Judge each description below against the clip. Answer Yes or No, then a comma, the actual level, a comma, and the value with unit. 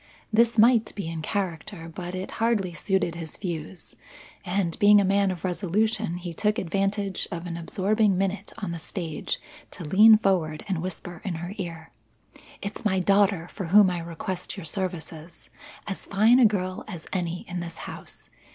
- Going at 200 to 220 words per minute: No, average, 170 wpm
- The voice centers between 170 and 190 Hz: Yes, medium, 185 Hz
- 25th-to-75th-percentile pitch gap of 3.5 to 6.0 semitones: No, average, 3.1 semitones